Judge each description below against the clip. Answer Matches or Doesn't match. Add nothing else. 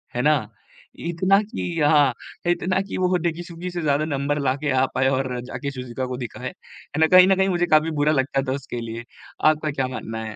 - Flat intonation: Doesn't match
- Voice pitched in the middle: Matches